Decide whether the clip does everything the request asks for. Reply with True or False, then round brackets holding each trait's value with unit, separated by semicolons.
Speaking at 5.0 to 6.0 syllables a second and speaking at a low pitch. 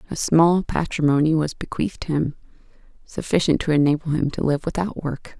False (5.3 syllables/s; 155 Hz)